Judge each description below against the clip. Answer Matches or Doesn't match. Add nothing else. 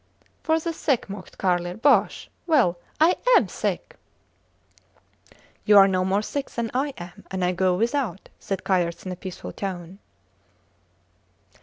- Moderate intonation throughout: Doesn't match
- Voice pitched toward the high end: Matches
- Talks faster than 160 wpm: Doesn't match